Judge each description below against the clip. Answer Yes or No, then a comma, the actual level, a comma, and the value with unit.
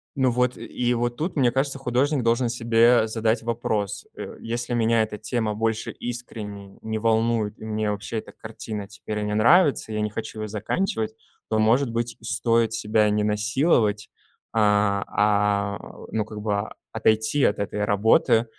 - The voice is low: Yes, low, 110 Hz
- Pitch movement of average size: No, narrow, 2.0 semitones